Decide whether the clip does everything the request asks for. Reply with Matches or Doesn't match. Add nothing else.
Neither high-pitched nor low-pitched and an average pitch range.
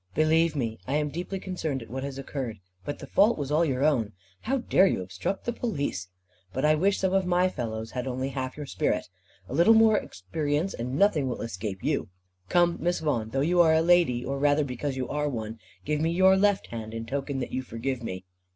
Doesn't match